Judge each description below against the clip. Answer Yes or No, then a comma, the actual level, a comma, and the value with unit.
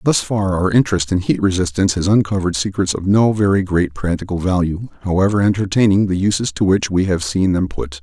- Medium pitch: No, very low, 95 Hz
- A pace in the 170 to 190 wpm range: No, average, 200 wpm